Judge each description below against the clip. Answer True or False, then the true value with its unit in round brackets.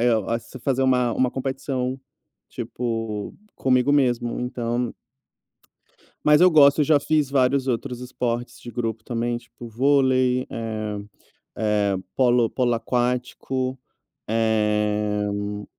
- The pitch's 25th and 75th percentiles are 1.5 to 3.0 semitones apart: True (2.5 semitones)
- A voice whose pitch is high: False (120 Hz)